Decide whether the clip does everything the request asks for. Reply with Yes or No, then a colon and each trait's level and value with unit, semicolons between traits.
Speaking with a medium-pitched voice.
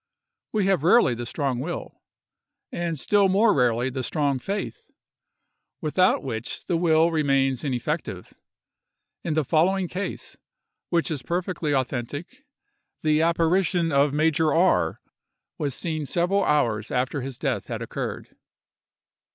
Yes: medium, 155 Hz